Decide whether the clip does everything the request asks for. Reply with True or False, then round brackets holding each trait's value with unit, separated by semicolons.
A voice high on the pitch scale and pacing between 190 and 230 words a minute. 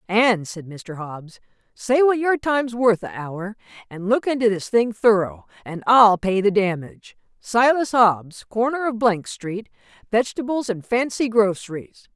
False (215 Hz; 155 wpm)